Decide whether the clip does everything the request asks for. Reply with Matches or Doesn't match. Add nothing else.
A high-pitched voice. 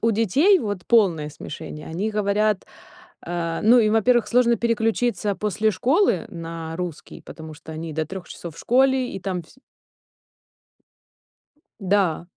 Matches